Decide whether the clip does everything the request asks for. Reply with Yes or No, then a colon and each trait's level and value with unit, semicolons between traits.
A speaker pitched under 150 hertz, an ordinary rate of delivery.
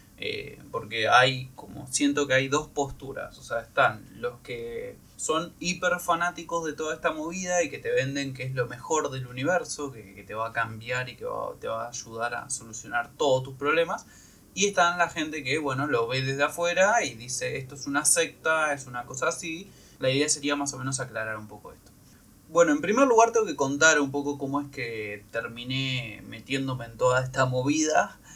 No: medium, 140 Hz; fast, 205 wpm